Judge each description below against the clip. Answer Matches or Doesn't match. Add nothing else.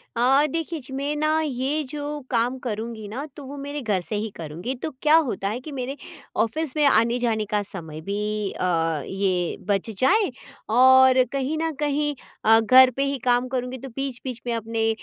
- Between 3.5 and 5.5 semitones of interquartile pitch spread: Matches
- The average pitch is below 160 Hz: Doesn't match